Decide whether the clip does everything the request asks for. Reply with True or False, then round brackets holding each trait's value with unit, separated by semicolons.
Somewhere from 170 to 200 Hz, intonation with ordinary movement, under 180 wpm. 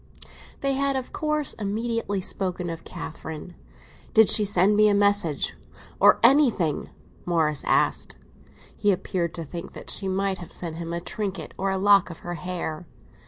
True (190 Hz; 3.4 semitones; 165 wpm)